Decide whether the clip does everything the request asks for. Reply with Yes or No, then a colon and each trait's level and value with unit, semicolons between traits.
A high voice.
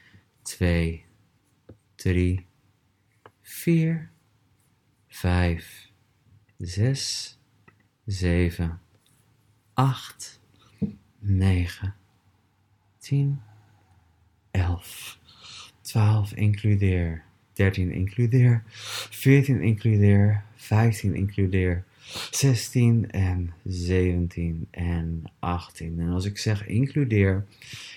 No: low, 105 Hz